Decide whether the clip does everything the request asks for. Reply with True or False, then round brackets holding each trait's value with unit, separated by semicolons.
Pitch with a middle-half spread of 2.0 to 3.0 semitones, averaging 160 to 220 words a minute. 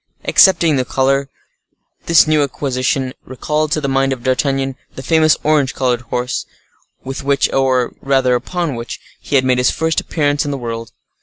True (2.6 semitones; 170 wpm)